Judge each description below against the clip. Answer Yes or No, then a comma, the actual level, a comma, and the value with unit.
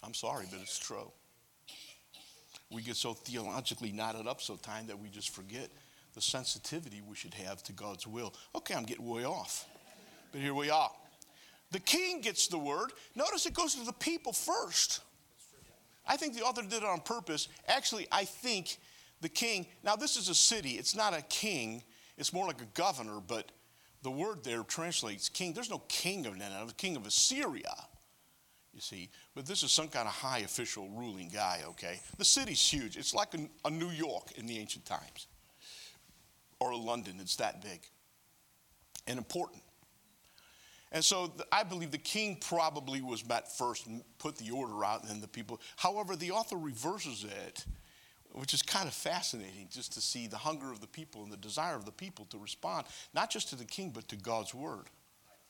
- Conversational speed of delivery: Yes, average, 190 wpm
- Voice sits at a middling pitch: Yes, medium, 145 Hz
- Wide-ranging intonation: Yes, wide, 8.9 semitones